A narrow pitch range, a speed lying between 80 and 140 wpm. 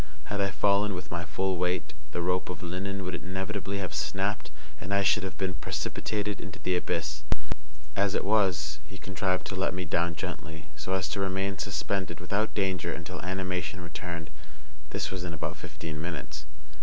No: narrow, 2.3 semitones; average, 180 wpm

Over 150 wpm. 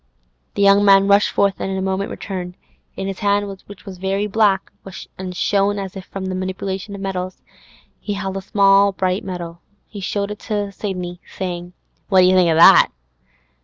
Yes: average, 190 wpm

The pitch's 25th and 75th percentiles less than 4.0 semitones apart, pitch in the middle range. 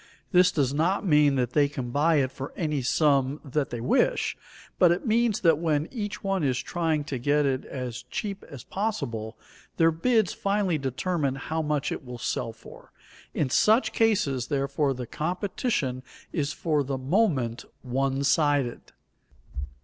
No: average, 5.0 semitones; medium, 145 Hz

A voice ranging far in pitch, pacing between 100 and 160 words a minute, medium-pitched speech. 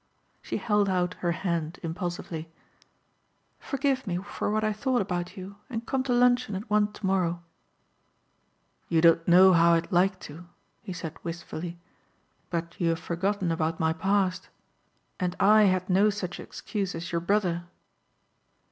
No: average, 3.3 semitones; average, 150 wpm; medium, 180 Hz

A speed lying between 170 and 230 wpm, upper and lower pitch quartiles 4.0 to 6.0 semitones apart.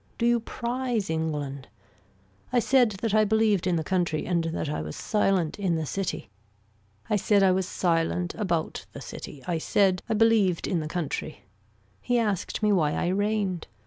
Yes: average, 175 wpm; average, 4.7 semitones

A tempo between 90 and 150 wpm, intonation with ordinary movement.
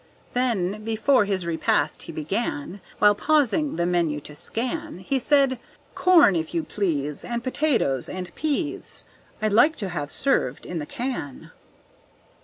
No: average, 145 wpm; wide, 7.9 semitones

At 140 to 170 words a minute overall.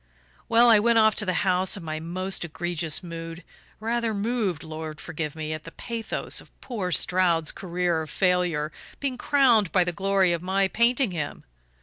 No: average, 180 wpm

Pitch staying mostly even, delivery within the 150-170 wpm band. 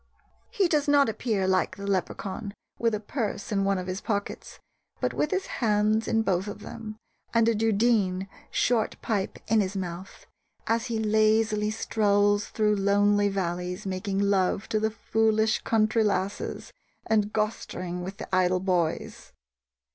Yes: narrow, 2.3 semitones; average, 155 wpm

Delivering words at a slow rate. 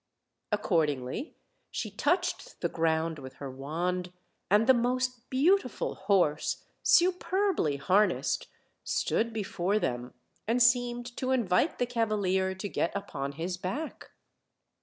Yes: slow, 115 wpm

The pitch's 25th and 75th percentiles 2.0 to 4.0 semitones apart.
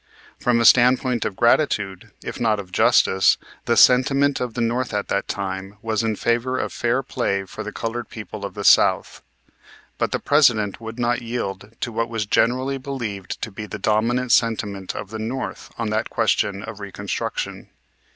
Yes: average, 3.1 semitones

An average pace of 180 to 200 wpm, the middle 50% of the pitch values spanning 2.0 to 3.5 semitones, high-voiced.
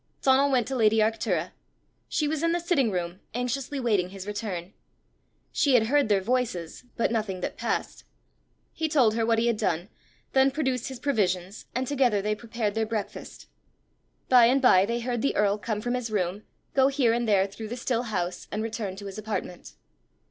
No: average, 190 wpm; average, 3.9 semitones; high, 225 Hz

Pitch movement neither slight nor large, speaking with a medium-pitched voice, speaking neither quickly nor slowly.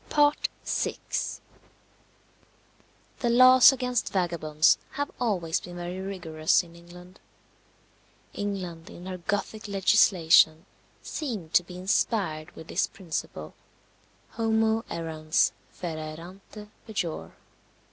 No: average, 4.4 semitones; medium, 180 Hz; slow, 95 wpm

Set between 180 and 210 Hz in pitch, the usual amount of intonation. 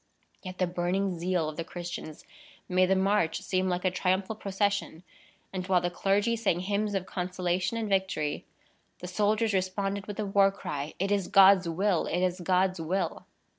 No: medium, 185 Hz; narrow, 1.9 semitones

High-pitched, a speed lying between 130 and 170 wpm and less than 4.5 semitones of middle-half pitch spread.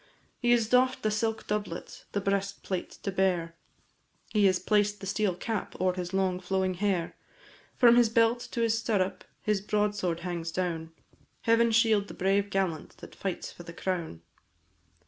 Yes: high, 195 Hz; average, 165 wpm; average, 3.0 semitones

